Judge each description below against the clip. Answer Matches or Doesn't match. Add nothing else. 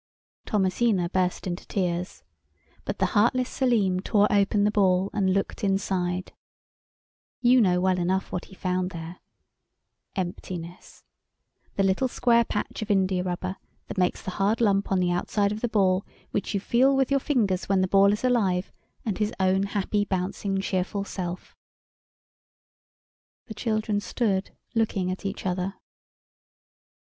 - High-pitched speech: Matches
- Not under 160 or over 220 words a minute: Doesn't match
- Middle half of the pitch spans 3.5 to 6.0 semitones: Doesn't match